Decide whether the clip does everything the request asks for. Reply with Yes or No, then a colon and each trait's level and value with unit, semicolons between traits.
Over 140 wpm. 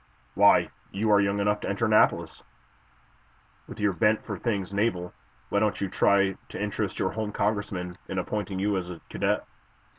Yes: average, 175 wpm